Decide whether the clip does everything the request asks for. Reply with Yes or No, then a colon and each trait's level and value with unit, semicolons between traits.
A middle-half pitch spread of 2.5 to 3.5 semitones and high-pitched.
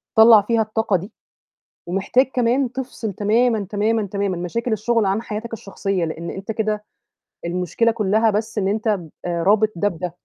Yes: average, 2.8 semitones; high, 210 Hz